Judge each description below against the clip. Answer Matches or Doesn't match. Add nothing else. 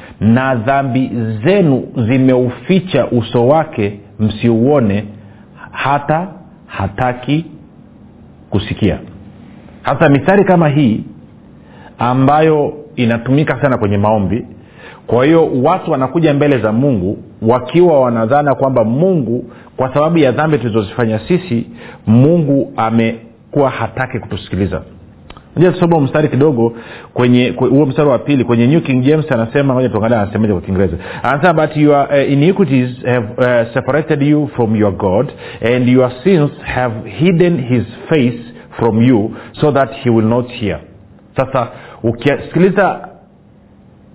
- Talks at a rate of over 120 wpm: Doesn't match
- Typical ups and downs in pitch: Matches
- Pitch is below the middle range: Matches